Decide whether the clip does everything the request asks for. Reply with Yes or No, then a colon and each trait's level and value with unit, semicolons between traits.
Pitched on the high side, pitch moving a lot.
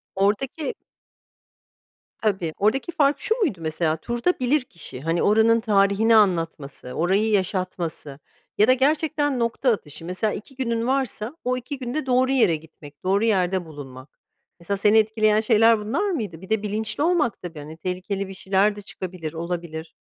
Yes: high, 210 Hz; wide, 5.8 semitones